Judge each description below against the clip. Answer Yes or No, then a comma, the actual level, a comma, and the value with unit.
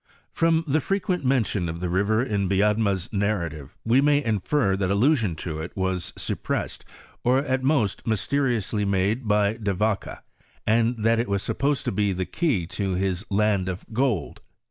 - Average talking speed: Yes, average, 175 wpm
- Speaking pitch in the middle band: No, low, 105 Hz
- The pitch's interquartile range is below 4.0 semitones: No, average, 4.9 semitones